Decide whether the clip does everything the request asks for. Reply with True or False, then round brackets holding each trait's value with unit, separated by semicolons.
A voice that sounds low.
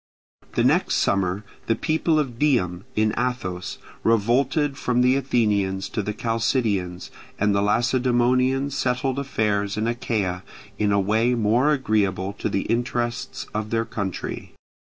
True (115 Hz)